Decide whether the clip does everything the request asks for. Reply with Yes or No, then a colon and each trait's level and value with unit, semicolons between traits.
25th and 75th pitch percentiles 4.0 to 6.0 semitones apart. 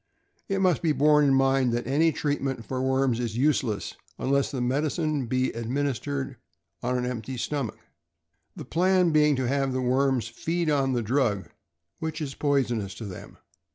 No: average, 3.3 semitones